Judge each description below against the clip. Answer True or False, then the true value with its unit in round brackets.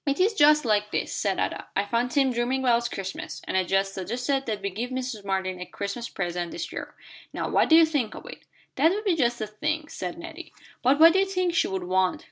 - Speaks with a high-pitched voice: True (240 Hz)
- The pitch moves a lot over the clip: True (7.5 semitones)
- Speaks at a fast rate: True (245 wpm)